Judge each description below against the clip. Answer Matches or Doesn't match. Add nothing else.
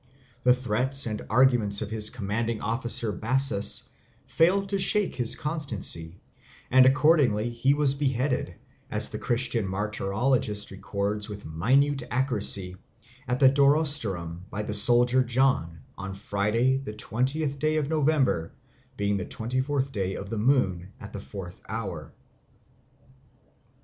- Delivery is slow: Matches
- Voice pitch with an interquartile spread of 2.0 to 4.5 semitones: Doesn't match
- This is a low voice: Matches